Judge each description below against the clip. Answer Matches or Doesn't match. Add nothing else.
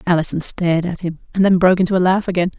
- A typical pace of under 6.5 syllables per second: Doesn't match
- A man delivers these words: Doesn't match